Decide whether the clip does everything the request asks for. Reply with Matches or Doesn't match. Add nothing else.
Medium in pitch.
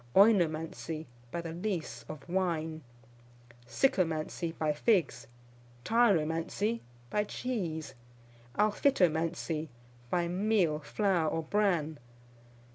Matches